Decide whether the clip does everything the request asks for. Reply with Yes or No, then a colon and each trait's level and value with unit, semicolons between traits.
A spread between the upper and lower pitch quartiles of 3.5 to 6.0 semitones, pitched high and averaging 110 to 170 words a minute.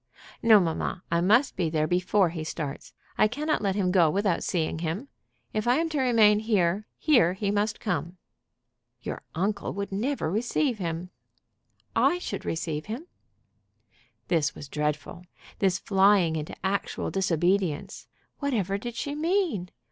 Yes: average, 4.7 semitones; high, 195 Hz; average, 150 wpm